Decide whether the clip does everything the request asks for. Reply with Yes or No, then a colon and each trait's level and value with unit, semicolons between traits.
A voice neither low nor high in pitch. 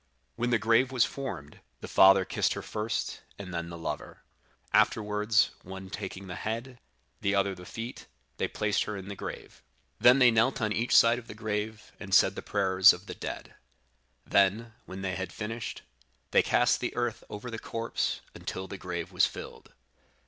No: low, 105 Hz